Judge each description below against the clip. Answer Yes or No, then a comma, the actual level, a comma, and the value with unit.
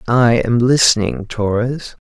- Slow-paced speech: Yes, slow, 115 wpm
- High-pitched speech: No, low, 120 Hz